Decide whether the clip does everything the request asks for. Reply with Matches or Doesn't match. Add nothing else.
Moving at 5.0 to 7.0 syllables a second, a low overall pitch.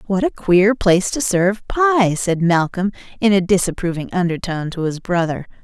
Doesn't match